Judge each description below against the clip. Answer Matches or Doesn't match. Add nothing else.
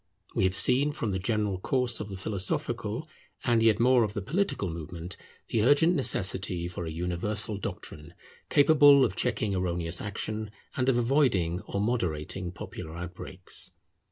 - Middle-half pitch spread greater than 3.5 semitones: Matches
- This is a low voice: Matches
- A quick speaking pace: Doesn't match